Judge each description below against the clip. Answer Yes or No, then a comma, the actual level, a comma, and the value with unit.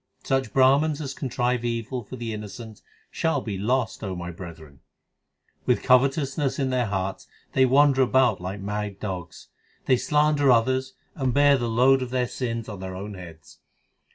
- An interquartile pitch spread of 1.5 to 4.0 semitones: No, average, 4.5 semitones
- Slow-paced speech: No, average, 165 wpm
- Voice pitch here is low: Yes, low, 125 Hz